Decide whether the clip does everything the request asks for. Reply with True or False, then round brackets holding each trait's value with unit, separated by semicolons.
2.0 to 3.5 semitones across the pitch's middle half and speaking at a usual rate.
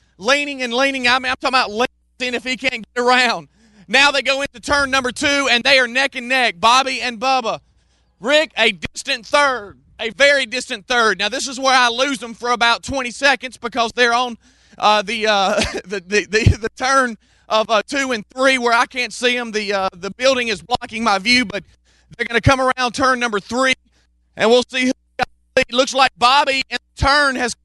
False (2.8 semitones; 215 wpm)